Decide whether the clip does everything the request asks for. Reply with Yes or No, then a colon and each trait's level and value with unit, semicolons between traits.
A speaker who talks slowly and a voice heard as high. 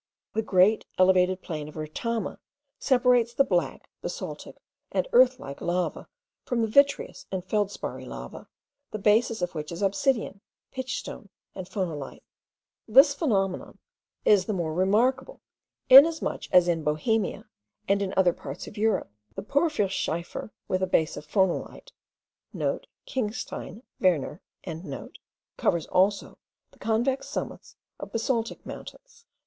Yes: slow, 125 wpm; high, 205 Hz